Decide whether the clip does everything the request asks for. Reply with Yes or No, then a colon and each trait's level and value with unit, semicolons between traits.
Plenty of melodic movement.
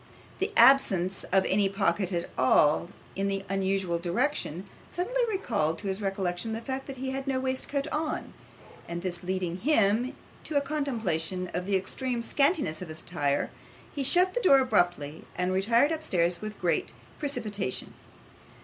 Yes: wide, 7.2 semitones